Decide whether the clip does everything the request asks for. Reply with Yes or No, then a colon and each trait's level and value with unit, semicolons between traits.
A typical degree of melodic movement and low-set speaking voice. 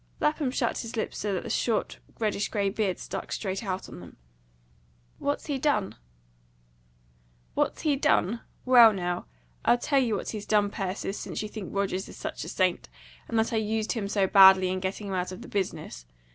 No: average, 3.3 semitones; high, 205 Hz